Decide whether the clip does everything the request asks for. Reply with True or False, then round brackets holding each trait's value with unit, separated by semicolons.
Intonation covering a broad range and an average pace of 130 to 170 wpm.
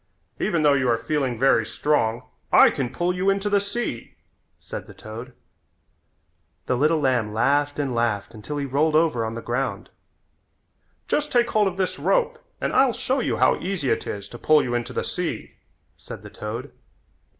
False (7.4 semitones; 185 wpm)